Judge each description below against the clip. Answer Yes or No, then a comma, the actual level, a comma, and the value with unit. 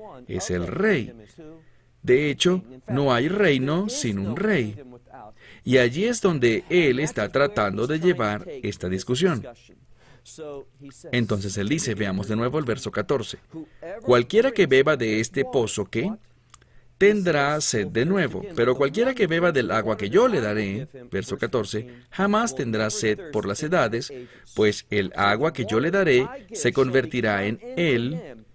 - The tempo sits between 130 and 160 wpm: Yes, average, 150 wpm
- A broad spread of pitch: Yes, wide, 6.7 semitones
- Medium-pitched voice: No, low, 125 Hz